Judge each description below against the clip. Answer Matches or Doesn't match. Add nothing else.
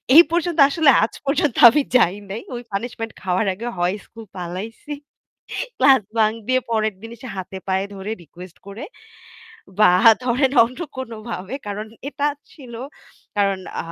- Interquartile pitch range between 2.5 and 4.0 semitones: Doesn't match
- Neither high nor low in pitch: Doesn't match